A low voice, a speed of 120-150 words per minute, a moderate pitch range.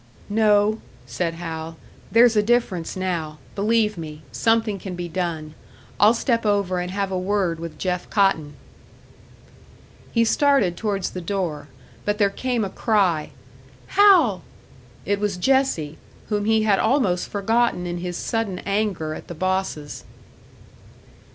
No: high, 195 Hz; average, 140 wpm; average, 4.0 semitones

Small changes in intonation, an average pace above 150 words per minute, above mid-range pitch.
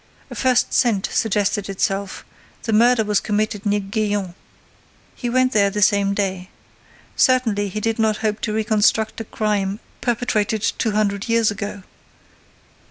No: narrow, 1.8 semitones; average, 145 wpm; high, 210 Hz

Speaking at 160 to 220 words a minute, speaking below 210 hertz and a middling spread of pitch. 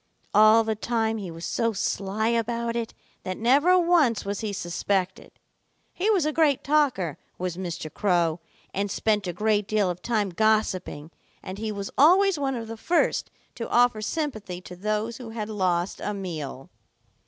No: average, 170 wpm; high, 215 Hz; average, 4.0 semitones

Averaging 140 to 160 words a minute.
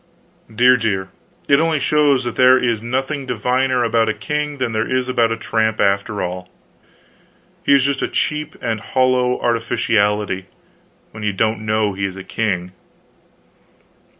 Yes: average, 155 wpm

